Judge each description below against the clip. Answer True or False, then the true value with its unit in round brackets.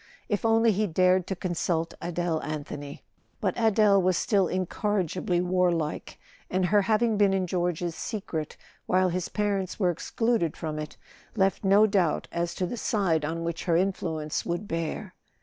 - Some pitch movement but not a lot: True (3.1 semitones)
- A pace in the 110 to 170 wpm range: True (160 wpm)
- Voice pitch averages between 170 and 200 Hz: True (185 Hz)